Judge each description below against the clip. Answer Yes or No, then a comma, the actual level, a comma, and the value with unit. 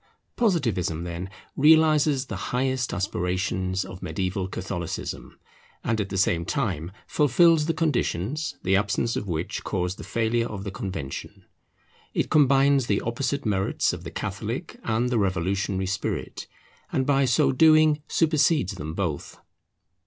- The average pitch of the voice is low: Yes, low, 110 Hz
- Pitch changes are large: Yes, wide, 7.1 semitones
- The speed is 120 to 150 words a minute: Yes, average, 140 wpm